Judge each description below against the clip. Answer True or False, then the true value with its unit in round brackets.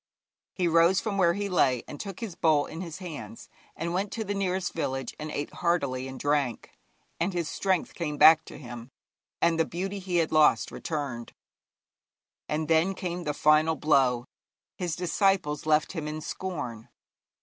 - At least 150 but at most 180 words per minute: True (170 wpm)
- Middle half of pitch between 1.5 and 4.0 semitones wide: True (3.6 semitones)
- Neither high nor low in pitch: True (160 Hz)